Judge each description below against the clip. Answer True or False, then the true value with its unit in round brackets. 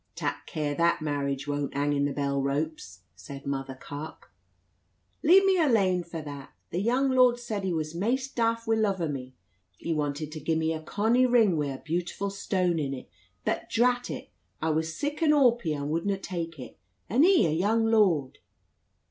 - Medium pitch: True (170 Hz)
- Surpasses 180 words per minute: True (190 wpm)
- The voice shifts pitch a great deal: True (7.6 semitones)